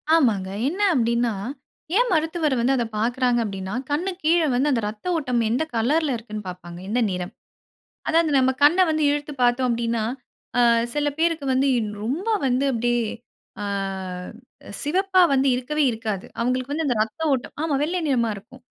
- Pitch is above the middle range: Yes, very high, 255 Hz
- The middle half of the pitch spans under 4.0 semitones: No, average, 4.8 semitones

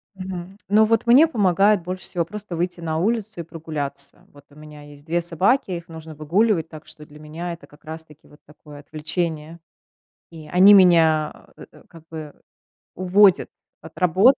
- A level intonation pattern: No, average, 3.5 semitones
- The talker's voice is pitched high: No, medium, 170 Hz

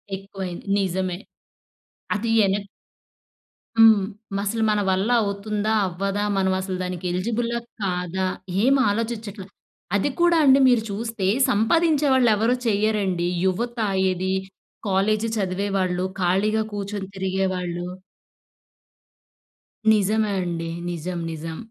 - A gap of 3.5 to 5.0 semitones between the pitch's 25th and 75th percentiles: No, average, 2.9 semitones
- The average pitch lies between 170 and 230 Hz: Yes, high, 200 Hz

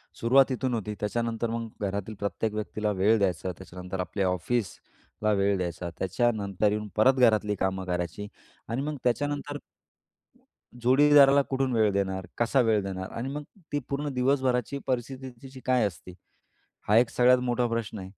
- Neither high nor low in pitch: No, low, 115 Hz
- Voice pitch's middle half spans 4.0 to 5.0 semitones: Yes, average, 4.5 semitones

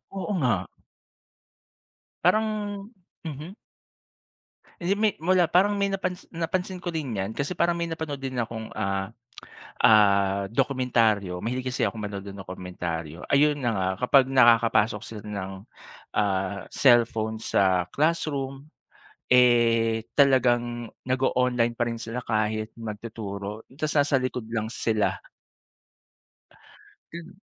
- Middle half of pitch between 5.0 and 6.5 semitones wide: Yes, wide, 5.5 semitones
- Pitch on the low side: Yes, low, 120 Hz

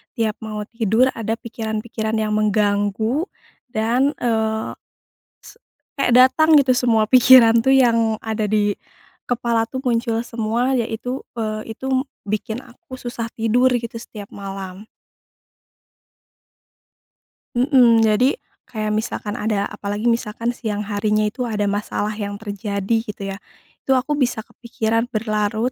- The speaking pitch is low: No, high, 225 Hz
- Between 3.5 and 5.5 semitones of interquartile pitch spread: No, narrow, 2.5 semitones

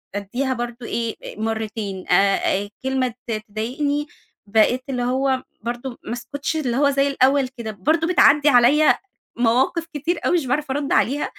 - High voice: Yes, very high, 255 Hz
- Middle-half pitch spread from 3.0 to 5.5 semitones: Yes, average, 3.7 semitones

